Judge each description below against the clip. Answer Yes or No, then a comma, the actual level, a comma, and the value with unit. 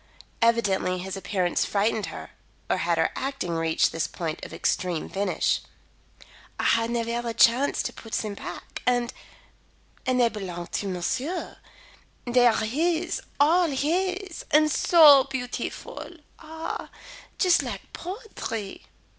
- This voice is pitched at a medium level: No, high, 240 Hz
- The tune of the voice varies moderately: No, wide, 7.5 semitones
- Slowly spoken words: Yes, slow, 130 wpm